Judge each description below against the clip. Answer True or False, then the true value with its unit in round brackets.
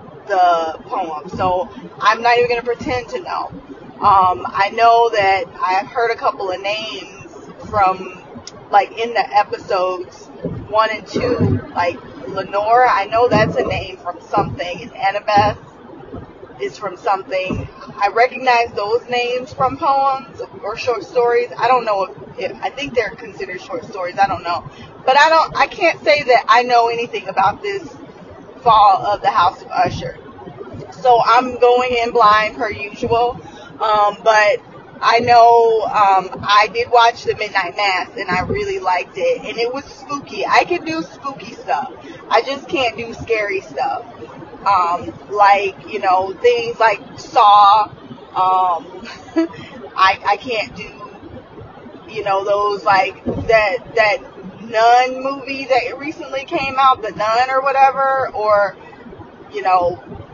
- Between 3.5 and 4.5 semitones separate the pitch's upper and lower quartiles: False (4.9 semitones)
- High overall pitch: True (225 Hz)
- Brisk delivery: False (150 wpm)